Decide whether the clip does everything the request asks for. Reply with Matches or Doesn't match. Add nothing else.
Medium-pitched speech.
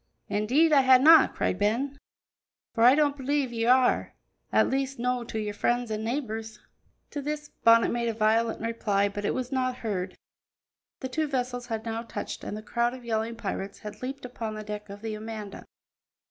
Doesn't match